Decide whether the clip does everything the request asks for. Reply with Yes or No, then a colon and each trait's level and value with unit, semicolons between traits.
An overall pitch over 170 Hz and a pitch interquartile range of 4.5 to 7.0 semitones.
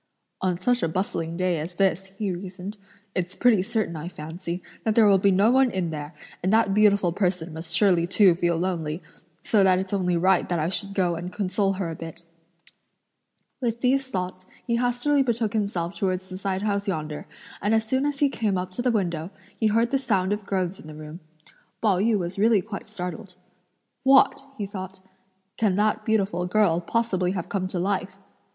No: high, 190 Hz; average, 3.3 semitones